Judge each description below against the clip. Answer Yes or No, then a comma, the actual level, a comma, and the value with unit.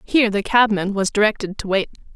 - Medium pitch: No, high, 205 Hz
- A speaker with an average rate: Yes, average, 195 wpm